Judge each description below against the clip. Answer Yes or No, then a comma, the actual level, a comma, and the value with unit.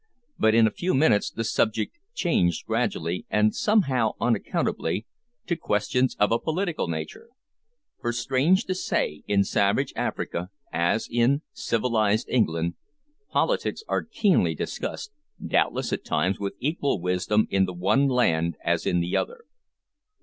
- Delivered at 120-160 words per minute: Yes, average, 140 wpm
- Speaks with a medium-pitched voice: No, low, 110 Hz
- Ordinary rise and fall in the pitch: No, wide, 7.3 semitones